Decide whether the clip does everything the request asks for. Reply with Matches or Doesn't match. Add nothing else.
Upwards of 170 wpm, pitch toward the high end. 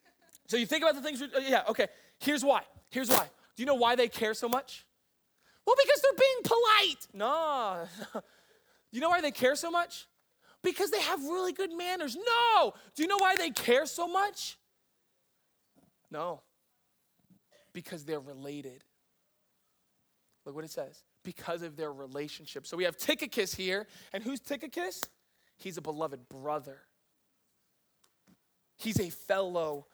Doesn't match